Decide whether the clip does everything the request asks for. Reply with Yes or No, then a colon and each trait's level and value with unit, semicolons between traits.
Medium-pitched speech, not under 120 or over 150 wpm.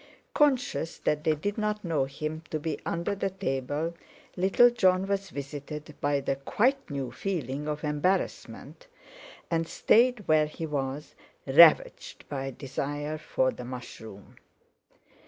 Yes: medium, 155 Hz; slow, 135 wpm